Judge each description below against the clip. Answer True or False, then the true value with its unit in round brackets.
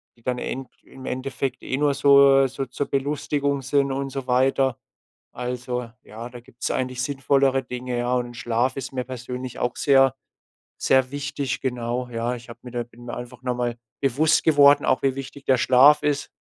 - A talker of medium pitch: False (130 Hz)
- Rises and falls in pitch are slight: True (2.0 semitones)